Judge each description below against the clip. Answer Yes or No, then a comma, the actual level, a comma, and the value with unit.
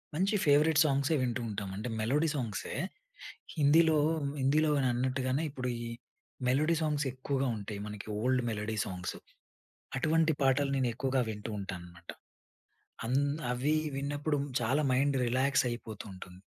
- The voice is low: Yes, low, 130 Hz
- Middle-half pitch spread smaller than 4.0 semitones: No, average, 4.3 semitones